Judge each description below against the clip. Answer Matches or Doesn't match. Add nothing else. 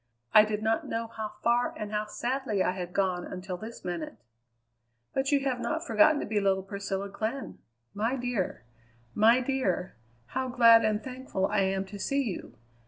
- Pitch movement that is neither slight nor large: Matches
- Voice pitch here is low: Doesn't match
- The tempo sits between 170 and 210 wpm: Matches